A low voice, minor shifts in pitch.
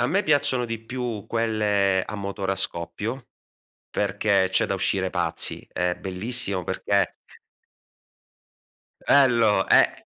No: low, 100 Hz; average, 3.6 semitones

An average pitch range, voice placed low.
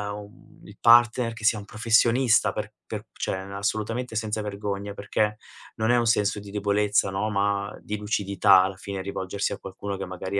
No: narrow, 1.8 semitones; low, 105 Hz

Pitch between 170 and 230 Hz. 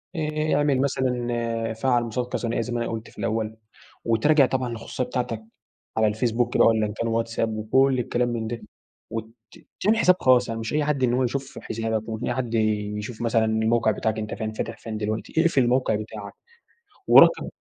No: low, 115 Hz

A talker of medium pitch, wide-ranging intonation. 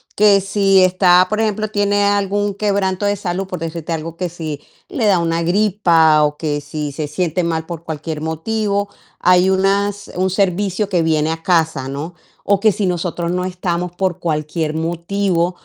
No: medium, 180 Hz; average, 3.5 semitones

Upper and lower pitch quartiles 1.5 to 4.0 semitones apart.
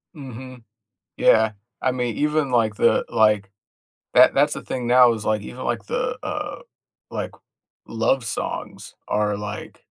Yes: average, 3.2 semitones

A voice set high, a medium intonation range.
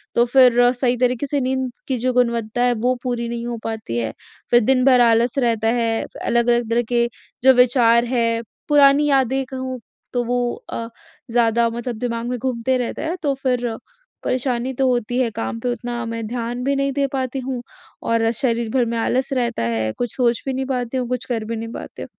No: high, 245 Hz; narrow, 1.8 semitones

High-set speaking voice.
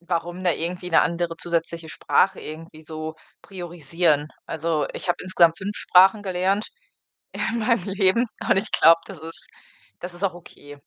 No: medium, 175 Hz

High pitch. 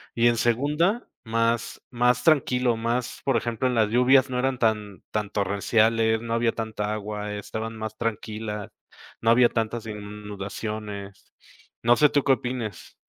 No: low, 115 Hz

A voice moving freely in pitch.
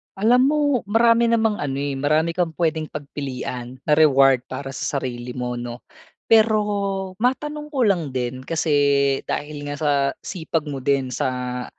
Yes: wide, 7.7 semitones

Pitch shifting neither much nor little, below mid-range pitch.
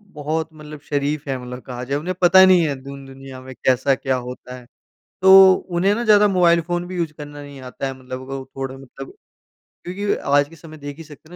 No: average, 4.5 semitones; medium, 145 Hz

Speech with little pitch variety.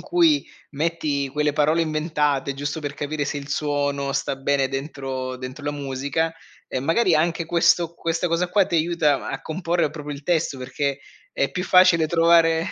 No: average, 3.0 semitones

